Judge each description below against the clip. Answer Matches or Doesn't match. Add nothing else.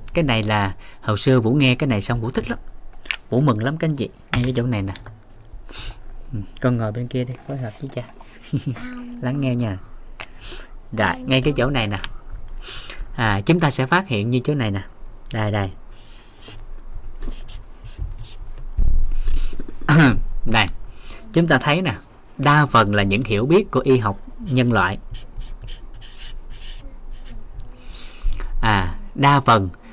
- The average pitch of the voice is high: Doesn't match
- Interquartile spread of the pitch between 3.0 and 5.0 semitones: Matches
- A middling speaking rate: Doesn't match